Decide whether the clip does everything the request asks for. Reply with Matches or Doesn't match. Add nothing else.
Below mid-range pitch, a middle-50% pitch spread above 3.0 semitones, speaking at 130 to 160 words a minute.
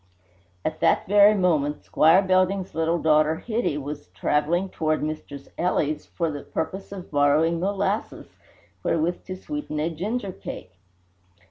Doesn't match